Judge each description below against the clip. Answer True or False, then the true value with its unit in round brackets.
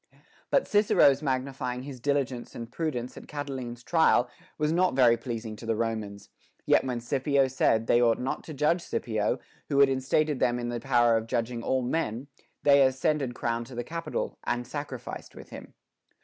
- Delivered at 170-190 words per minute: True (180 wpm)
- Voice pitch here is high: False (130 Hz)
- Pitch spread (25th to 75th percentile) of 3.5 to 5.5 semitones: False (3.1 semitones)